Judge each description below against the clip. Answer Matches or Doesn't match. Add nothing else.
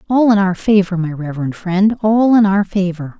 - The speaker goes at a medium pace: Matches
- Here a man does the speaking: Doesn't match